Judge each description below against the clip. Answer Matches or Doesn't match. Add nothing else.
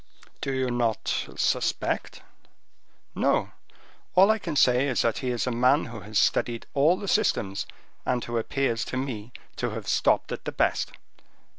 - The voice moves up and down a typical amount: Matches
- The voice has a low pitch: Matches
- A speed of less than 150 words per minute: Doesn't match